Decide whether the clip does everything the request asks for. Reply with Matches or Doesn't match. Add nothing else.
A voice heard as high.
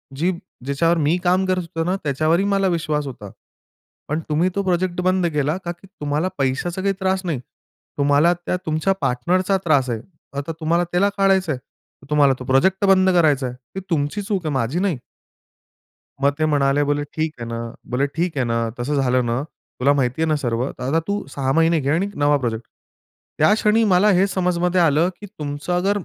Doesn't match